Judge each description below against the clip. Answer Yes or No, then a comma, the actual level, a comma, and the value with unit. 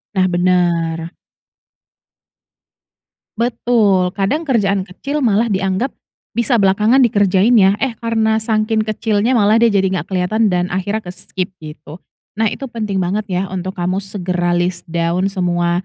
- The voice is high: Yes, high, 195 Hz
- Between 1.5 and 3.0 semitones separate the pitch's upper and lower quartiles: No, average, 3.5 semitones